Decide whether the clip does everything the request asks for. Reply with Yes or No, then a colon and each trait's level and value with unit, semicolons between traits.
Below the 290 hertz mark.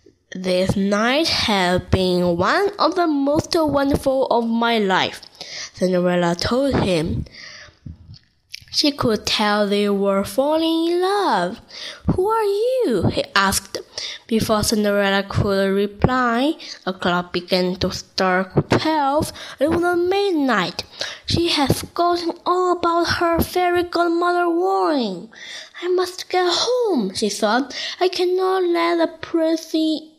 No: very high, 295 Hz